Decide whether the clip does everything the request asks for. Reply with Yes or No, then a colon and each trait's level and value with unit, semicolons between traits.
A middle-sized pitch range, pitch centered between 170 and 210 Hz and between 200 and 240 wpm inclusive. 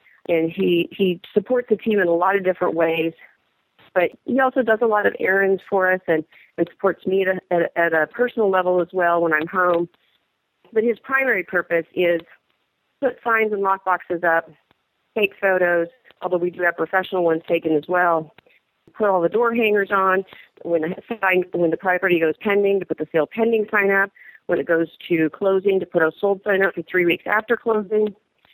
Yes: average, 3.3 semitones; medium, 185 Hz; fast, 205 wpm